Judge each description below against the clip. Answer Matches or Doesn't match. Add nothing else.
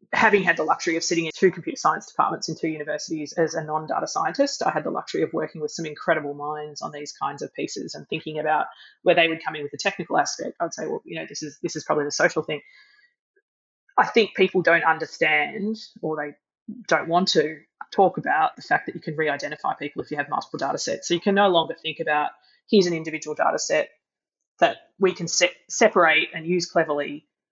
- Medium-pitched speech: Matches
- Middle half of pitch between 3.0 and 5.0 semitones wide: Matches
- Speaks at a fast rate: Matches